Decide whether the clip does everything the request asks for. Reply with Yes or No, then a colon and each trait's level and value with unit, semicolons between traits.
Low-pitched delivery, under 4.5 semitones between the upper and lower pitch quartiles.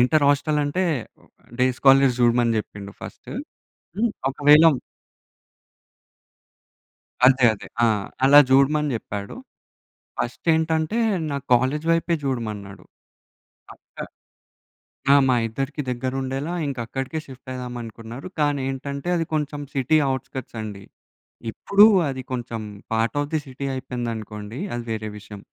Yes: low, 130 Hz; average, 3.9 semitones